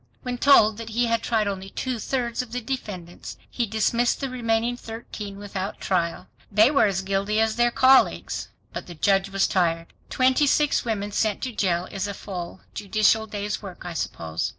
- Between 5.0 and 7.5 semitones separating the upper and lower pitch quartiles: No, average, 3.6 semitones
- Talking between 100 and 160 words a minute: No, average, 185 wpm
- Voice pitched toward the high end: Yes, high, 215 Hz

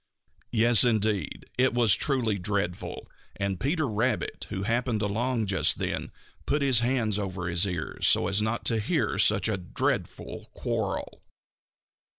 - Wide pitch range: No, average, 3.4 semitones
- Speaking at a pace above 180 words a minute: No, average, 145 wpm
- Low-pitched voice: Yes, low, 110 Hz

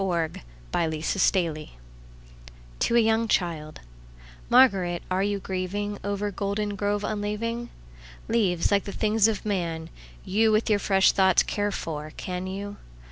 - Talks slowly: Yes, slow, 115 wpm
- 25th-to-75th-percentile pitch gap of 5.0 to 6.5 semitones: No, average, 3.7 semitones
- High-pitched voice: Yes, high, 195 Hz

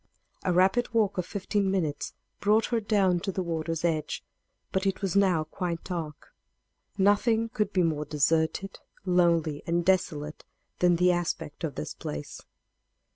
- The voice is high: No, medium, 180 Hz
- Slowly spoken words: No, average, 150 wpm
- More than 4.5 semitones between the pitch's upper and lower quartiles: No, average, 3.4 semitones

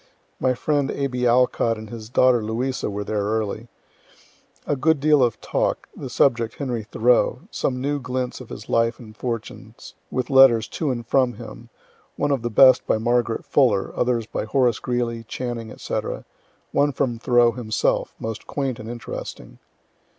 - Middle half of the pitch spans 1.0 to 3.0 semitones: Yes, narrow, 2.4 semitones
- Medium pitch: No, low, 120 Hz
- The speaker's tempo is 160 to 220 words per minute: Yes, average, 165 wpm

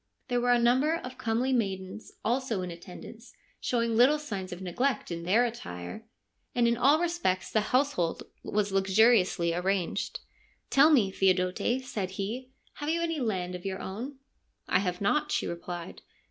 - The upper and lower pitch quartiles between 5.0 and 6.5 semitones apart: Yes, wide, 5.5 semitones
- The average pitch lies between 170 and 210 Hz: No, high, 220 Hz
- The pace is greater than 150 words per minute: Yes, average, 180 wpm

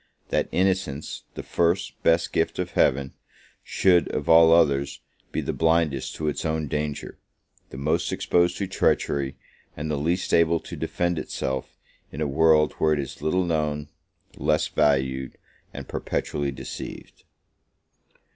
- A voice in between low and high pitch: No, very low, 75 Hz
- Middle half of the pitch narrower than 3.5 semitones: Yes, average, 2.9 semitones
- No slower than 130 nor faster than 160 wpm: Yes, average, 145 wpm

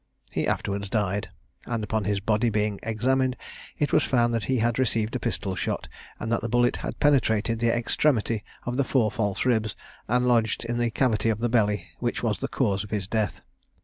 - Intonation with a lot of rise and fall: No, narrow, 2.5 semitones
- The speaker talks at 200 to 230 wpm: Yes, fast, 205 wpm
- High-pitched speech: No, low, 115 Hz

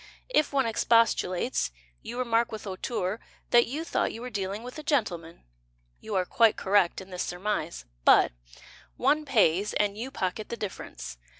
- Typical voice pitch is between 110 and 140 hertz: No, high, 215 Hz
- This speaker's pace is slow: No, average, 165 wpm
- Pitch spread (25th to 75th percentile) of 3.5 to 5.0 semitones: Yes, average, 4.4 semitones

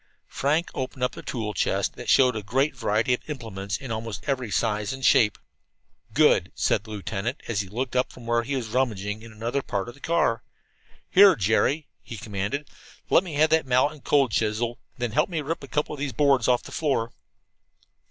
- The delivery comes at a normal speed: No, fast, 210 wpm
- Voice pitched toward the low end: Yes, low, 125 Hz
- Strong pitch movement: No, average, 4.2 semitones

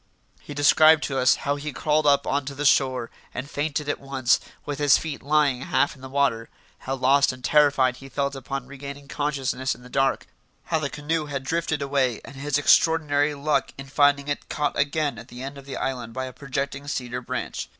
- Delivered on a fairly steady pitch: Yes, narrow, 1.7 semitones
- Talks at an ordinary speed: No, fast, 210 wpm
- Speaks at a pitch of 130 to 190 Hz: Yes, medium, 140 Hz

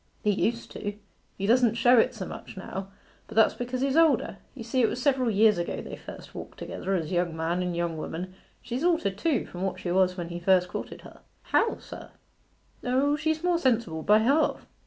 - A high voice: Yes, high, 220 Hz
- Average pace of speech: No, fast, 210 wpm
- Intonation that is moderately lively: No, wide, 5.9 semitones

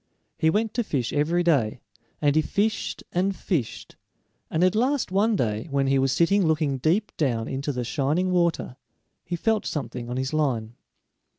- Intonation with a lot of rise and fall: Yes, wide, 5.7 semitones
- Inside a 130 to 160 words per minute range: No, average, 175 wpm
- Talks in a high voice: No, medium, 155 Hz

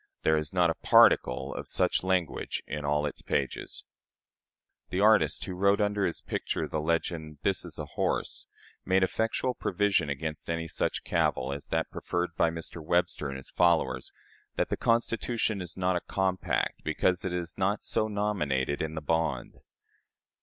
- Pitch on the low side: Yes, very low, 85 Hz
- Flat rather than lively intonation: No, average, 3.8 semitones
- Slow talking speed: No, average, 165 wpm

